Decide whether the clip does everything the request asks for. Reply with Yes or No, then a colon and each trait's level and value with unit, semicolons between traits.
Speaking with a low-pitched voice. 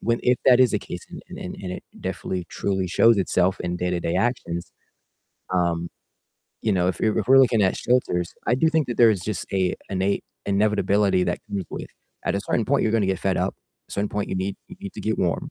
Yes: low, 100 Hz